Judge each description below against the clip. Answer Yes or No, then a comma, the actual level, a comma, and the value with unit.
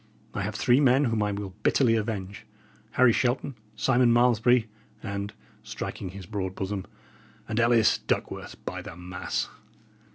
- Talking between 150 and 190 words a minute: No, average, 140 wpm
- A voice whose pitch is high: No, low, 110 Hz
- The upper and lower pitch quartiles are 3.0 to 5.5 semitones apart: Yes, average, 3.4 semitones